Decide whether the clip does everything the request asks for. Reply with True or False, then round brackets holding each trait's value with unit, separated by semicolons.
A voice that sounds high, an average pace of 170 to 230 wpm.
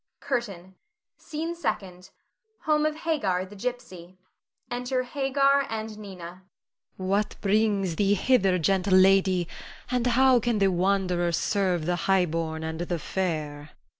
False (195 Hz; 135 wpm)